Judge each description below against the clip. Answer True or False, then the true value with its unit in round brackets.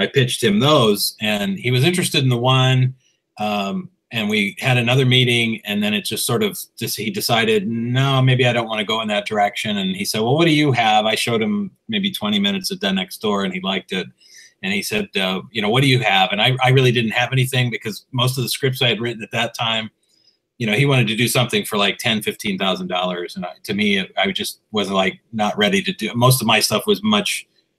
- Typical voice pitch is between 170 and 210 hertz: False (130 Hz)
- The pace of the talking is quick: True (255 wpm)